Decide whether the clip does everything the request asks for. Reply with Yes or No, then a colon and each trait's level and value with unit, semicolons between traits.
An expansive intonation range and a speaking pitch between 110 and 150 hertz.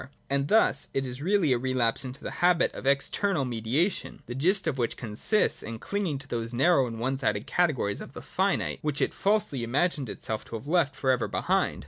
Yes: wide, 6.1 semitones; low, 135 Hz